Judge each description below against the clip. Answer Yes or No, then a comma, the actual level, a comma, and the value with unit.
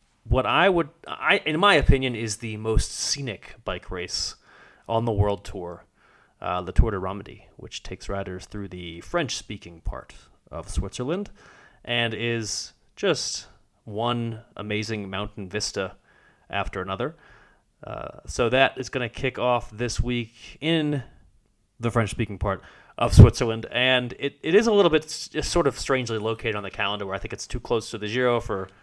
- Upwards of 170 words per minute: No, average, 165 wpm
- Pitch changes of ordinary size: Yes, average, 4.0 semitones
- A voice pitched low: Yes, low, 115 Hz